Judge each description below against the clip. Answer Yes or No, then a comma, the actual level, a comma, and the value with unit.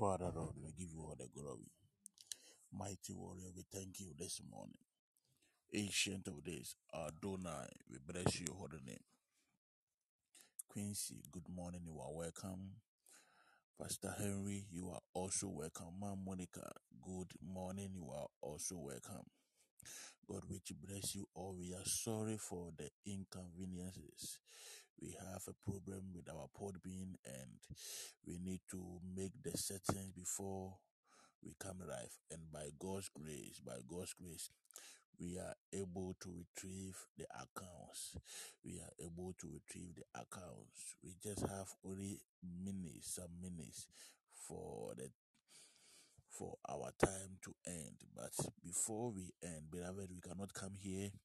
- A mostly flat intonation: Yes, narrow, 1.8 semitones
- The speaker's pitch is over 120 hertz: No, very low, 95 Hz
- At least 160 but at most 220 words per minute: No, average, 140 wpm